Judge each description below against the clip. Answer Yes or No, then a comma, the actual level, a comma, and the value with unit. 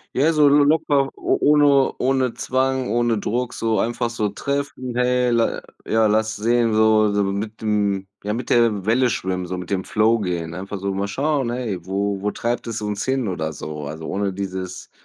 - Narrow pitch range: No, average, 4.1 semitones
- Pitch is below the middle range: Yes, low, 110 Hz